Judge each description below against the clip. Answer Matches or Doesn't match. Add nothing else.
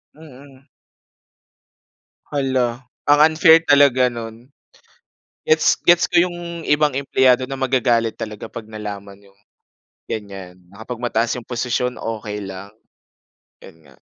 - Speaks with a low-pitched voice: Matches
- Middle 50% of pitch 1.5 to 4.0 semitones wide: Doesn't match